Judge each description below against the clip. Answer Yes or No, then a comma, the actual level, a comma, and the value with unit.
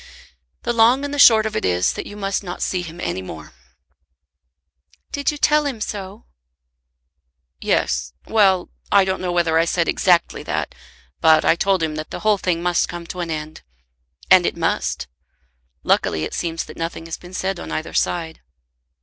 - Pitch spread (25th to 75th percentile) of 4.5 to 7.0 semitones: No, average, 4.1 semitones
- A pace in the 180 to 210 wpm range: Yes, average, 185 wpm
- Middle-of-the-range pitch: Yes, medium, 175 Hz